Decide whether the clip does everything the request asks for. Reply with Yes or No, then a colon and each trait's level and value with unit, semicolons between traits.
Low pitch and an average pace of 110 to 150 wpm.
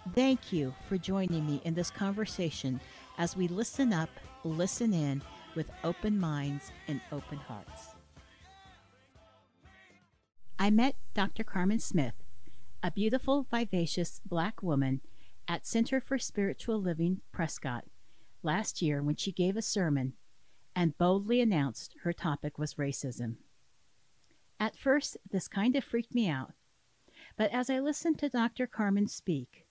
No: medium, 175 Hz; slow, 135 wpm